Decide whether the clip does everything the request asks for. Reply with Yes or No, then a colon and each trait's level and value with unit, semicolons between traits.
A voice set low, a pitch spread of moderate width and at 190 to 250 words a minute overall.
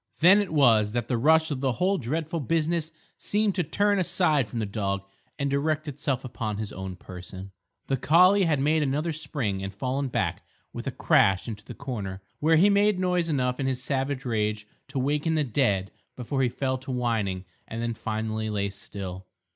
No: low, 130 Hz; wide, 6.6 semitones; average, 195 wpm